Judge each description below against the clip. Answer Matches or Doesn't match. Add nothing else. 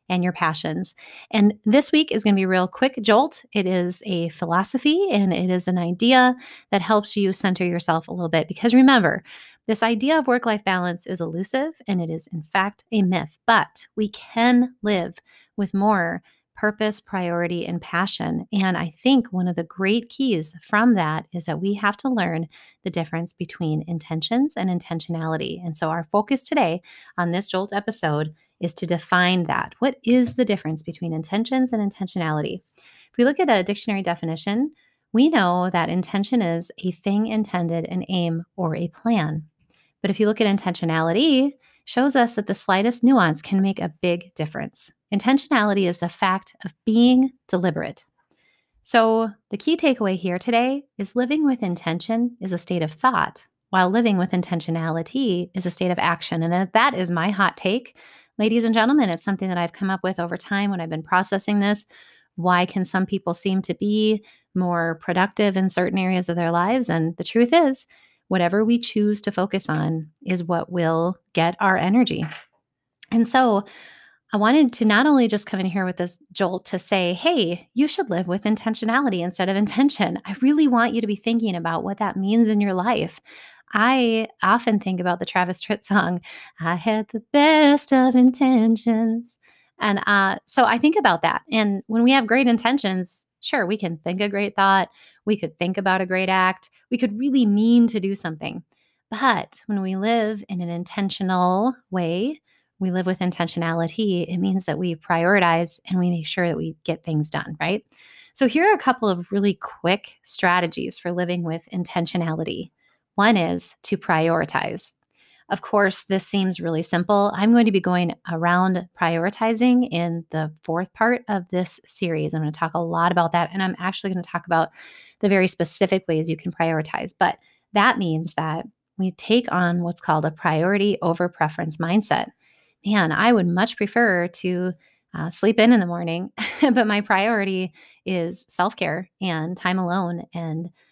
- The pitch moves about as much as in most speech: Matches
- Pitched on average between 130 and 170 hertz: Doesn't match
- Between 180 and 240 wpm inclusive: Matches